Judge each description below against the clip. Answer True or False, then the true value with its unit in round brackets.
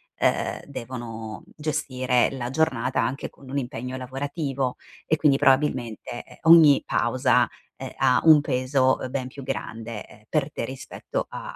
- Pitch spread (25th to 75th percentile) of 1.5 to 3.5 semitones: True (2.5 semitones)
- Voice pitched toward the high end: False (130 Hz)